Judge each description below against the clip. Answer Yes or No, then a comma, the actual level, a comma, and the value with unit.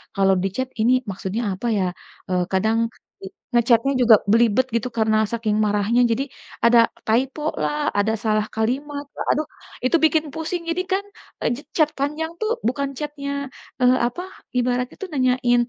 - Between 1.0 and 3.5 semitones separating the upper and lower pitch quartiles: No, average, 4.5 semitones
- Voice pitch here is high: Yes, high, 245 Hz